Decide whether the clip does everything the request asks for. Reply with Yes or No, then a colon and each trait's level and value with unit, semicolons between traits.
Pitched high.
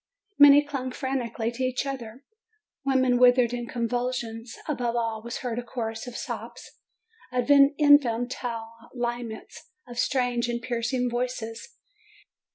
Yes: high, 245 Hz